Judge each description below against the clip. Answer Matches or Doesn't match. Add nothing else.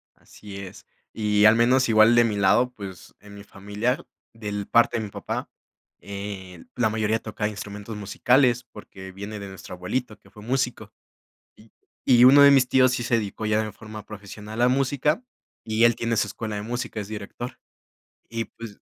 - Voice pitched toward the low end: Matches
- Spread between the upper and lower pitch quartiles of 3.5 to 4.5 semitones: Doesn't match